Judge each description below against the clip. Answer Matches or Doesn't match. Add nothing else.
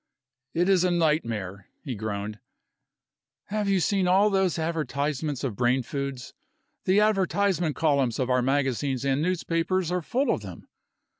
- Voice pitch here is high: Doesn't match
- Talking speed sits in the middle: Matches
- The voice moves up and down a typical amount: Doesn't match